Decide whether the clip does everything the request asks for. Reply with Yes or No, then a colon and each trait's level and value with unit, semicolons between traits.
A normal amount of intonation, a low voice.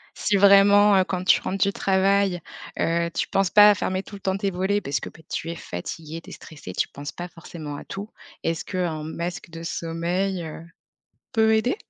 No: average, 3.1 semitones; medium, 185 Hz